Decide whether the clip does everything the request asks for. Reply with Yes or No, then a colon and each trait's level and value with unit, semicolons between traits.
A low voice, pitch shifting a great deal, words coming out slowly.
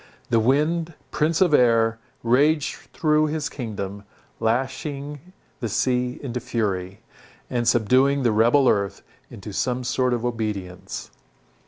No: low, 125 Hz; average, 4.2 semitones; slow, 125 wpm